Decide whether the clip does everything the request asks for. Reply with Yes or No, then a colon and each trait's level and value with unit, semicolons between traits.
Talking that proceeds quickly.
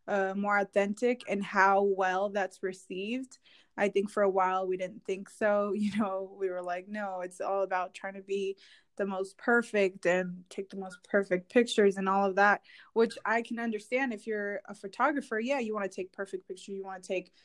Yes: fast, 210 wpm